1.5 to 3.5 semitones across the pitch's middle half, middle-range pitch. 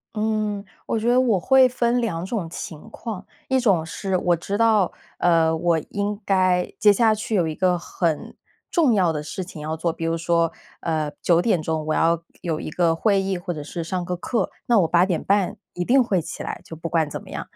No: average, 4.4 semitones; medium, 180 Hz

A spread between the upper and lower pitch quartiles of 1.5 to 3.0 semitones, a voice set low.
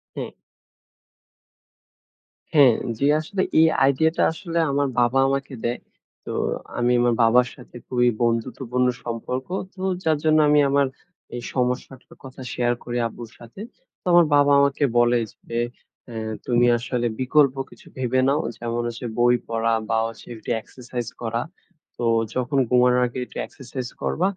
Yes: narrow, 2.6 semitones; low, 125 Hz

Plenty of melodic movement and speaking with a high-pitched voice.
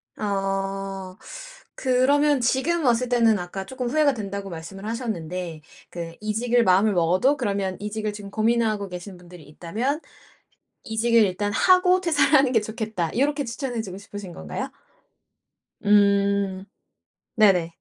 No: average, 4.2 semitones; high, 210 Hz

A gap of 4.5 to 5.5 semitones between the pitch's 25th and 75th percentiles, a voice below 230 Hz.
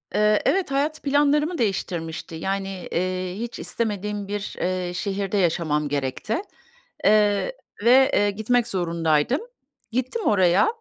Yes: average, 5.0 semitones; high, 205 Hz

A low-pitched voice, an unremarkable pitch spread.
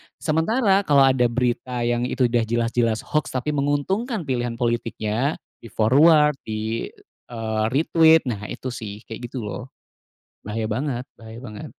Yes: low, 120 Hz; average, 4.1 semitones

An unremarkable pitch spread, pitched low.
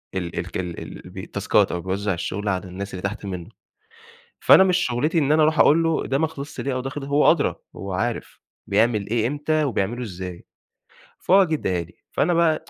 No: wide, 8.2 semitones; low, 120 Hz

